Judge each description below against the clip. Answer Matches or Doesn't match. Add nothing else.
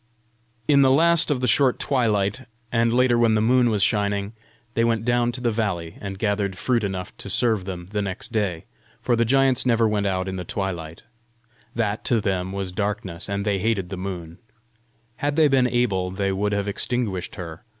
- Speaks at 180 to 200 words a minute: Matches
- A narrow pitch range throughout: Doesn't match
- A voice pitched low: Matches